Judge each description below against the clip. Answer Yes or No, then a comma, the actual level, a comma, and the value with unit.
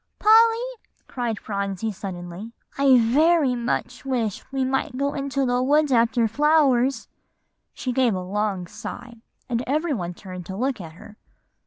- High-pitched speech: Yes, high, 245 Hz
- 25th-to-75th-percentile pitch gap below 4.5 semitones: No, average, 4.9 semitones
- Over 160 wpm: No, average, 150 wpm